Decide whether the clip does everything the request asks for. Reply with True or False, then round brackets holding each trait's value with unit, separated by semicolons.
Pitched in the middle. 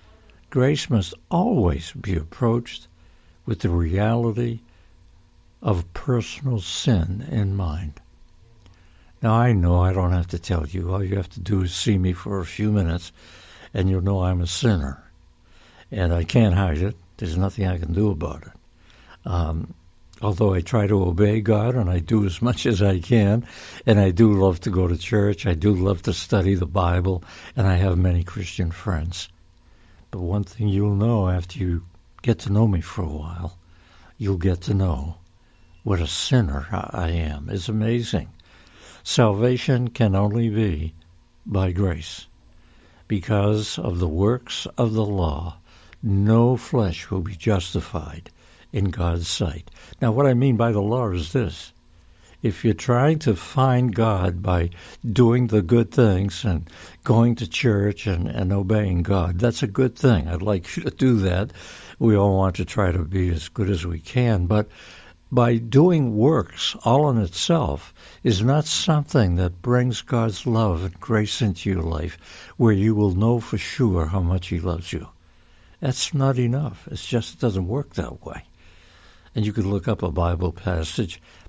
False (95 Hz)